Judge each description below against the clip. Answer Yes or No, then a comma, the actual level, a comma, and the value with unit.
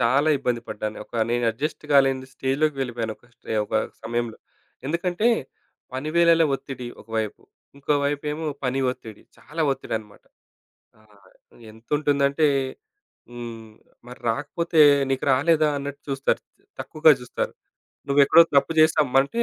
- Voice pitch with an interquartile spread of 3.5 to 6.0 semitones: Yes, average, 4.2 semitones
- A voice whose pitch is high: No, low, 135 Hz